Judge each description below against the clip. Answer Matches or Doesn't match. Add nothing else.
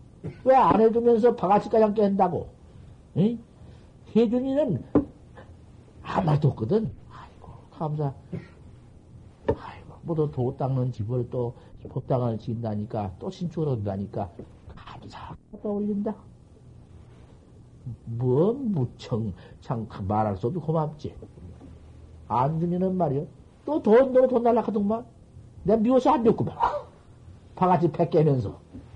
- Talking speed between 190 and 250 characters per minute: Matches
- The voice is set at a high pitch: Doesn't match